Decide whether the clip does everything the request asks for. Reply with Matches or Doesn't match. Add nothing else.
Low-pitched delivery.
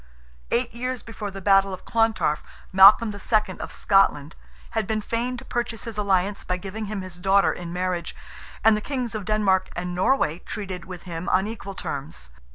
Doesn't match